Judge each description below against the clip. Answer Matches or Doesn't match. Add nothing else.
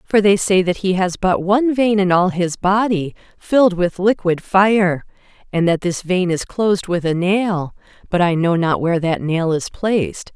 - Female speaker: Matches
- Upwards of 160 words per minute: Matches